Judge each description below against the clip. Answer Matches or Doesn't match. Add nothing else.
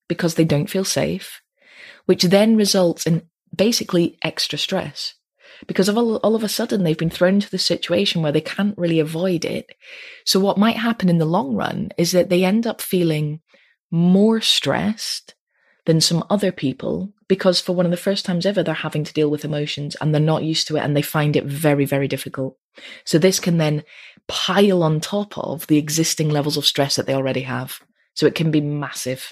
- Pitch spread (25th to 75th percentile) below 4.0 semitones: Doesn't match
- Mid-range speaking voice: Matches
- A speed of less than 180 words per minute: Doesn't match